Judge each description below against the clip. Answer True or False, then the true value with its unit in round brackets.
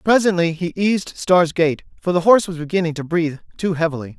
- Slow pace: False (200 wpm)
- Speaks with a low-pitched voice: False (170 Hz)